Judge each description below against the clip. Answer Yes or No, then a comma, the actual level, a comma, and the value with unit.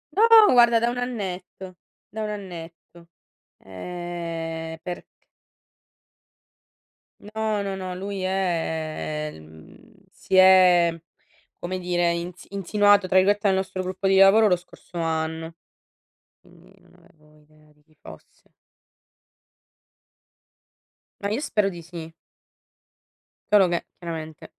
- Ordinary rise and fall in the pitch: Yes, average, 3.4 semitones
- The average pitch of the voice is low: No, medium, 180 Hz